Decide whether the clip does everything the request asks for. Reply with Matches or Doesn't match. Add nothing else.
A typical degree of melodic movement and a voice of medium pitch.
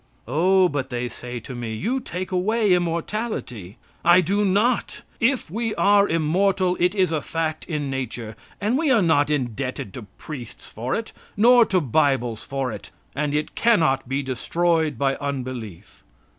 Doesn't match